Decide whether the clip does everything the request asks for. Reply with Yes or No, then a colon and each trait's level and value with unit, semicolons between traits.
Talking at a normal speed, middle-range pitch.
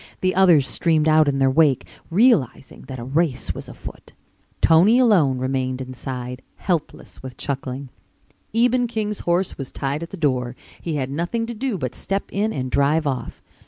Yes: average, 170 wpm; medium, 150 Hz